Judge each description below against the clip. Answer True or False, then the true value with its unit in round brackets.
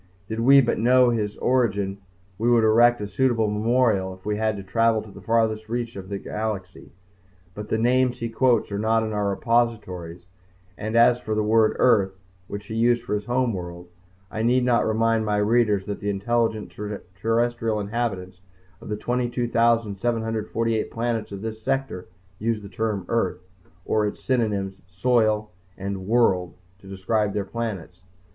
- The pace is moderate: True (165 wpm)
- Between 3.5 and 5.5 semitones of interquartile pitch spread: False (2.6 semitones)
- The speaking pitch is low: True (110 Hz)